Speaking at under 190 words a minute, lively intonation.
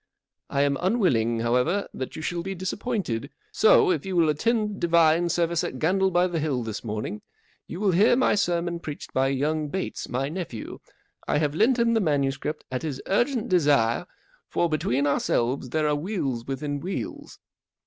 Yes: average, 180 wpm; wide, 5.8 semitones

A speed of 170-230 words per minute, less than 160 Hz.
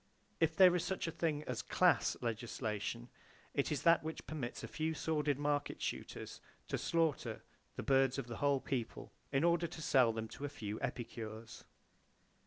Yes: average, 175 wpm; medium, 140 Hz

